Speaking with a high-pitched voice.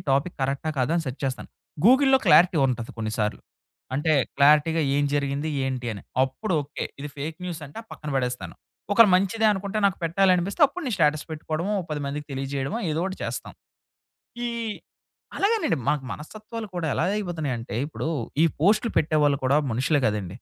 No: medium, 150 Hz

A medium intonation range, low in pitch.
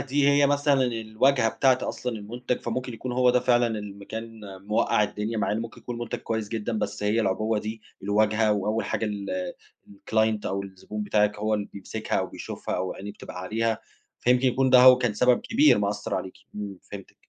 Yes: average, 3.1 semitones; low, 110 Hz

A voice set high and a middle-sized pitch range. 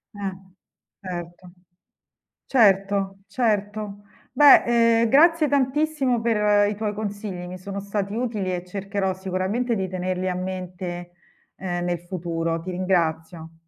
Yes: high, 195 Hz; average, 3.1 semitones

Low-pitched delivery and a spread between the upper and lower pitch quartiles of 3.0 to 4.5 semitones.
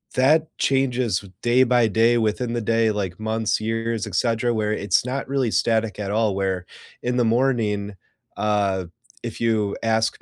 No: low, 115 Hz; narrow, 2.5 semitones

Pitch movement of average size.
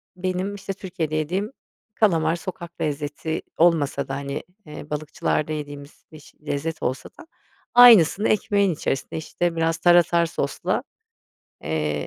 Yes: average, 3.9 semitones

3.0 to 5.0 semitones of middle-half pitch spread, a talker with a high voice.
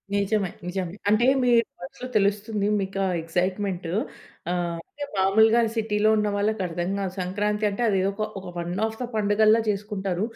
No: narrow, 2.5 semitones; high, 200 Hz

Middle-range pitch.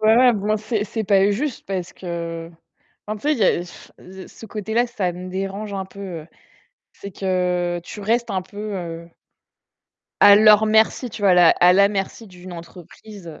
No: high, 195 Hz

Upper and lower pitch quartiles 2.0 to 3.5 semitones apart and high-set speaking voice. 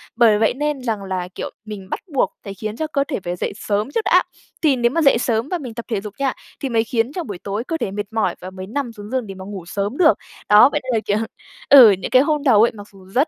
No: average, 4.9 semitones; high, 225 Hz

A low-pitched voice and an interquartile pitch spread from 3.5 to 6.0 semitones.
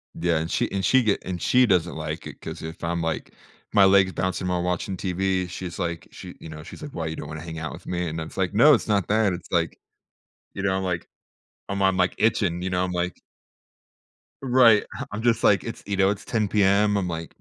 No: very low, 95 Hz; average, 3.1 semitones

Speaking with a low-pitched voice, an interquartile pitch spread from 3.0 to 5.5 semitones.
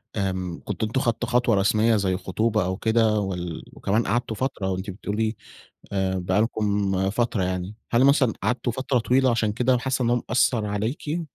Yes: low, 110 Hz; average, 3.6 semitones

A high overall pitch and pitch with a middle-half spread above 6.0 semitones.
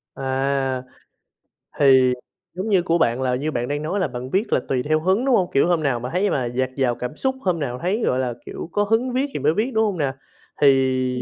No: medium, 145 Hz; wide, 6.5 semitones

